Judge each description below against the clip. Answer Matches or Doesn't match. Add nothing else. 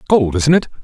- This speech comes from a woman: Doesn't match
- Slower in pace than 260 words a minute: Matches